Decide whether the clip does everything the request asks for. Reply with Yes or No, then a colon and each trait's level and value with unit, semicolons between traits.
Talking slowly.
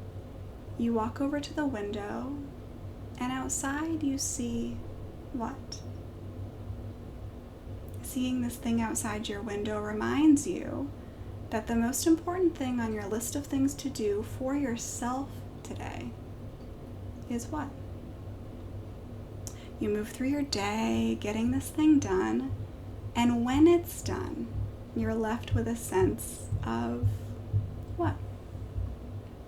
Yes: slow, 115 wpm